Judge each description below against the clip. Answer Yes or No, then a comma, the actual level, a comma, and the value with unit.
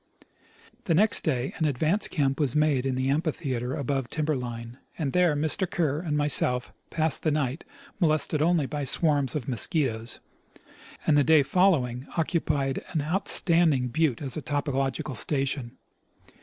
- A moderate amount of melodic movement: Yes, average, 3.1 semitones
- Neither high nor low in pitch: Yes, medium, 145 Hz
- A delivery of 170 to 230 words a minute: No, average, 155 wpm